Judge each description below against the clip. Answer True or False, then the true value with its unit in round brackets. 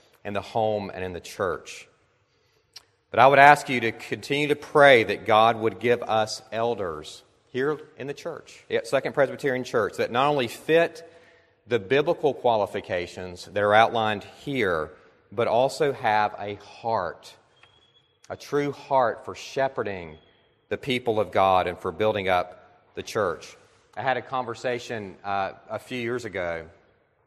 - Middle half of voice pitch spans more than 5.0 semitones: True (5.6 semitones)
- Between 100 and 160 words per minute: True (155 wpm)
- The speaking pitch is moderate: False (115 Hz)